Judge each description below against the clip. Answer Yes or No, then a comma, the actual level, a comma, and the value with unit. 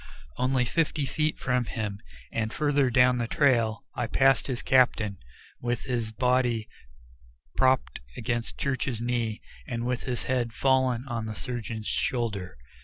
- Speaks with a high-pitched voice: No, low, 120 Hz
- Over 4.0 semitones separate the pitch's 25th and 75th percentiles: No, narrow, 2.4 semitones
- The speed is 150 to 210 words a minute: No, average, 140 wpm